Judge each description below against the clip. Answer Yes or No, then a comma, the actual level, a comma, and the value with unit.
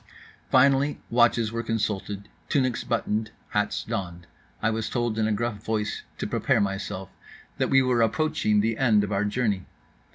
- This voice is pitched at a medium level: No, low, 110 Hz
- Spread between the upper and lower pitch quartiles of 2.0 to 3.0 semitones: Yes, narrow, 2.5 semitones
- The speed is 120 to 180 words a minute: Yes, average, 160 wpm